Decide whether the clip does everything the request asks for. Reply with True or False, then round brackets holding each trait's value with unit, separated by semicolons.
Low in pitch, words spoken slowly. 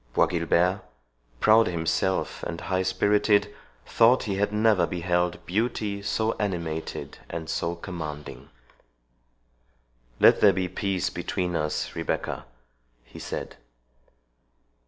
True (95 Hz; 110 wpm)